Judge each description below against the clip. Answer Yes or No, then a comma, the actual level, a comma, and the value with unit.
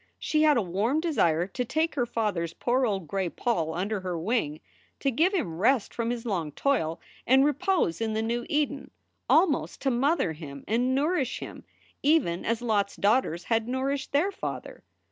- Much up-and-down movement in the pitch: Yes, wide, 6.8 semitones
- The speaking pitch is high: Yes, high, 235 Hz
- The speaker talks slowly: No, average, 185 wpm